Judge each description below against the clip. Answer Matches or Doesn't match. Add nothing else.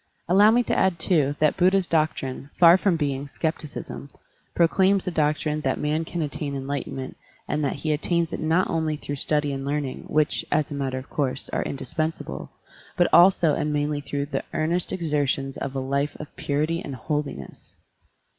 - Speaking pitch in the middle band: Matches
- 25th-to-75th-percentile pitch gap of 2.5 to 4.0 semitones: Matches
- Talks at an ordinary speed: Matches